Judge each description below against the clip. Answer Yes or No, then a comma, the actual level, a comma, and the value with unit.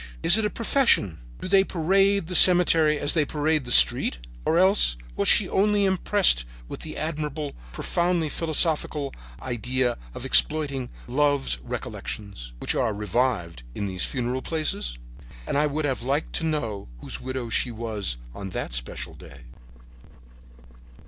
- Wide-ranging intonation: Yes, wide, 6.4 semitones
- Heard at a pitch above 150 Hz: No, medium, 145 Hz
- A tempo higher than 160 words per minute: No, average, 150 wpm